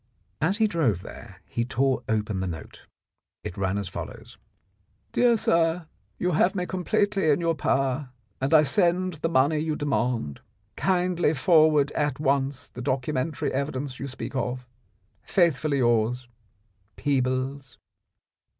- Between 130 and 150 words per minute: Yes, average, 140 wpm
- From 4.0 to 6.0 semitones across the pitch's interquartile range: Yes, average, 4.5 semitones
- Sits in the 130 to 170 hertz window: Yes, medium, 140 Hz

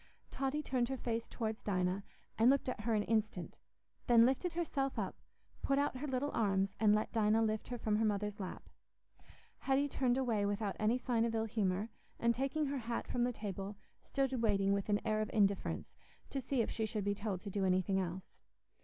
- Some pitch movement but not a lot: Yes, average, 3.8 semitones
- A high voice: Yes, high, 220 Hz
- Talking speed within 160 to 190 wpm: No, fast, 205 wpm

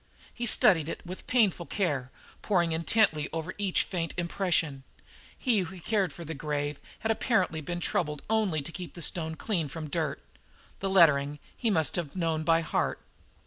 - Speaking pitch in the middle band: Yes, medium, 170 Hz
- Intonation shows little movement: No, average, 3.6 semitones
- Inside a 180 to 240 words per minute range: No, average, 170 wpm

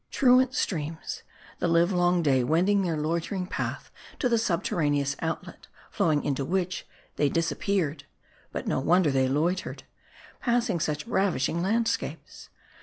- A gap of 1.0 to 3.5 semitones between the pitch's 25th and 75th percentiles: No, average, 4.4 semitones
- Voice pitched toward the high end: No, medium, 170 Hz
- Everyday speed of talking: No, slow, 125 wpm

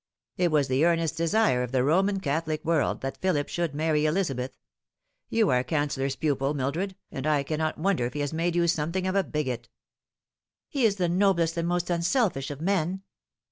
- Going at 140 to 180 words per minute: No, average, 190 wpm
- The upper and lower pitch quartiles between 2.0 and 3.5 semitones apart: No, average, 4.0 semitones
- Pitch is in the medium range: Yes, medium, 160 Hz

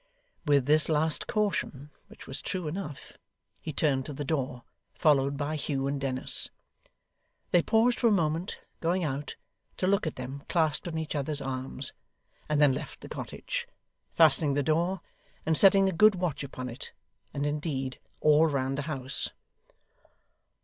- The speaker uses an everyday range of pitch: Yes, average, 3.3 semitones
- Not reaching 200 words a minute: Yes, average, 160 wpm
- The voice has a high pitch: No, medium, 150 Hz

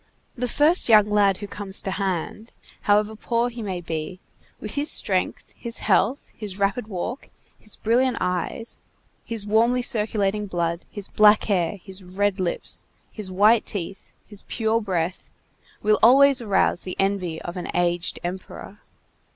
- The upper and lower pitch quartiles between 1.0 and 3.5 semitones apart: Yes, average, 3.2 semitones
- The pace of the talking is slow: No, average, 150 wpm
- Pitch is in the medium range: No, high, 205 Hz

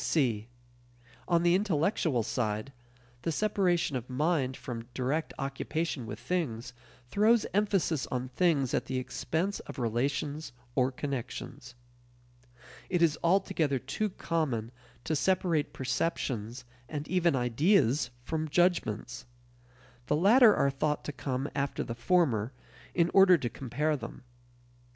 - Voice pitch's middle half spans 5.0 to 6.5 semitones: Yes, average, 5.3 semitones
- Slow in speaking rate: Yes, slow, 125 wpm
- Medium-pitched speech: Yes, medium, 145 Hz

